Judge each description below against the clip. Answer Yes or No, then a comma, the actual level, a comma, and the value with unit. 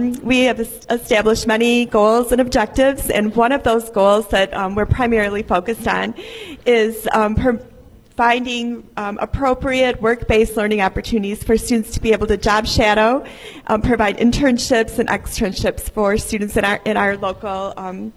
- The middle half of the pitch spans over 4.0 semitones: No, narrow, 2.4 semitones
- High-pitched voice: Yes, high, 225 Hz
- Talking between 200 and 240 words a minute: No, average, 160 wpm